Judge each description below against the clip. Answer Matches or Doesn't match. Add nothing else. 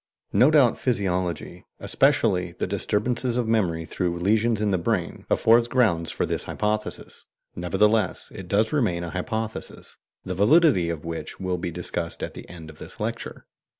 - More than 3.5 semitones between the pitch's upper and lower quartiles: Matches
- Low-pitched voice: Matches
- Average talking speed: Matches